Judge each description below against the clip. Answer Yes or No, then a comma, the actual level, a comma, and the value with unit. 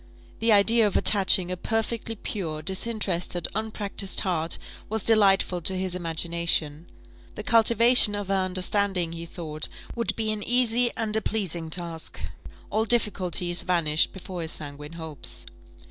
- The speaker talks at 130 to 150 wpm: Yes, average, 140 wpm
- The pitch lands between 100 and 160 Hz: No, high, 190 Hz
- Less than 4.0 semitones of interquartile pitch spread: No, average, 4.4 semitones